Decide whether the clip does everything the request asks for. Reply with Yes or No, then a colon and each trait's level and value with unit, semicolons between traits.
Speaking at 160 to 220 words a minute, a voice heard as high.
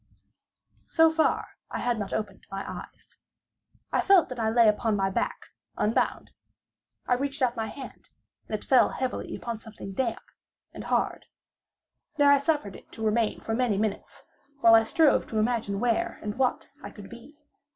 Yes: average, 170 wpm; high, 230 Hz